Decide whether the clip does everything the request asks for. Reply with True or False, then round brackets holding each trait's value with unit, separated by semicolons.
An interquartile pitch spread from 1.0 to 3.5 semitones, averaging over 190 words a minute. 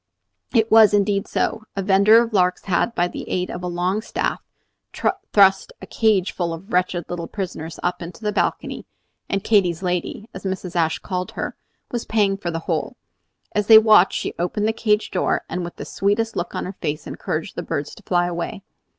True (3.1 semitones; 200 wpm)